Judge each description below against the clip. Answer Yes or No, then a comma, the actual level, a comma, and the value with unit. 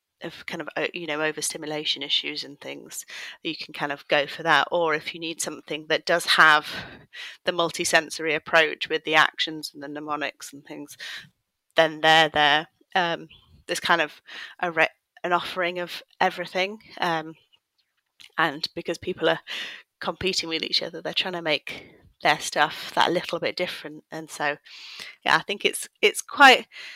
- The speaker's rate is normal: Yes, average, 165 wpm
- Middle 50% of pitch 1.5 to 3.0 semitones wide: Yes, narrow, 2.4 semitones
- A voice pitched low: No, medium, 160 Hz